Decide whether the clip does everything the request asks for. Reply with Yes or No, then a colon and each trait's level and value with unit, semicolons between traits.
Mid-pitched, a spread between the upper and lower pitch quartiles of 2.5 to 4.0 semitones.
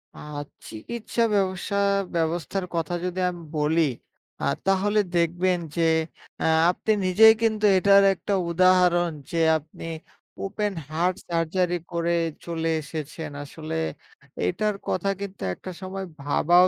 Yes: medium, 180 Hz; average, 2.8 semitones